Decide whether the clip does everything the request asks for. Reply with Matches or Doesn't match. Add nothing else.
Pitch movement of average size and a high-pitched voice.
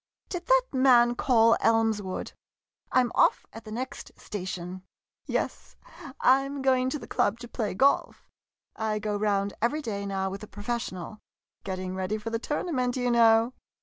Matches